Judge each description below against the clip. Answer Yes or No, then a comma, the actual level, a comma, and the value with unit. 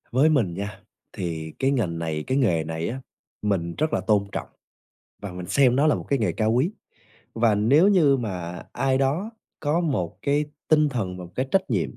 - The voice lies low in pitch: Yes, low, 115 Hz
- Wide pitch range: Yes, wide, 7.7 semitones